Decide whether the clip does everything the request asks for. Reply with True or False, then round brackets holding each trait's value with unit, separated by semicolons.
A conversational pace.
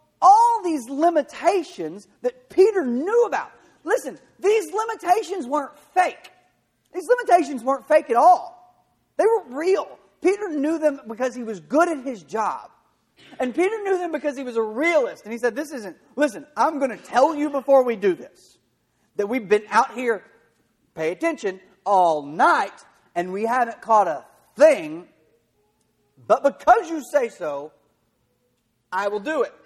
True (160 wpm)